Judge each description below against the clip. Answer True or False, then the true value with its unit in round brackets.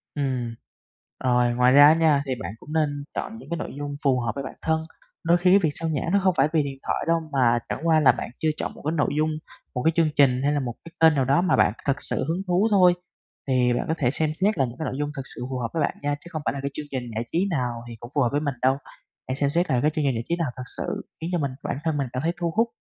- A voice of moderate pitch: True (145 Hz)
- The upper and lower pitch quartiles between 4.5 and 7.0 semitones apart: False (3.9 semitones)